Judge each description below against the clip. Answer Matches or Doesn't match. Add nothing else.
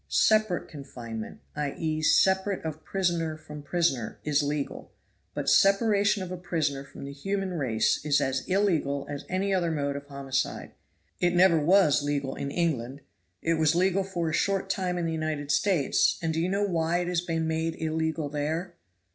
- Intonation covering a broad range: Doesn't match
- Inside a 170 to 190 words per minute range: Matches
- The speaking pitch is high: Doesn't match